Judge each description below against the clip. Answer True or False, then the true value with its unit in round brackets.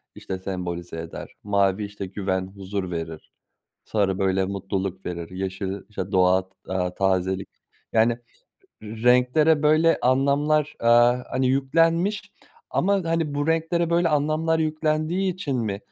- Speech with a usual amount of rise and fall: False (8.4 semitones)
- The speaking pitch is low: True (110 Hz)